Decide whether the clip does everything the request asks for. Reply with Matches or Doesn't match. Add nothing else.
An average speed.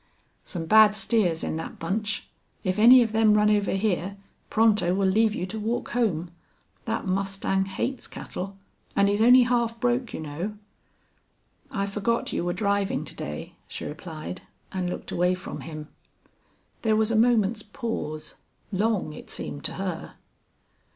Matches